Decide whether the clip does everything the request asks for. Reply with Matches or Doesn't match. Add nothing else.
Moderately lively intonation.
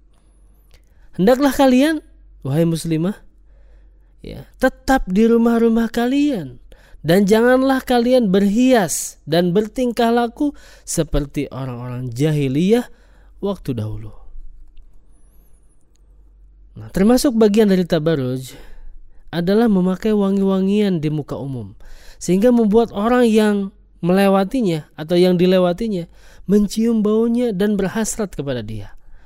Doesn't match